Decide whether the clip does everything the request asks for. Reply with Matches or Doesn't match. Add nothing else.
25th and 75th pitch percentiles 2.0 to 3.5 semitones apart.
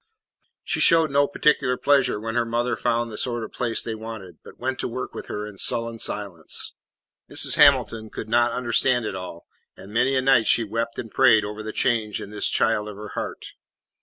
Matches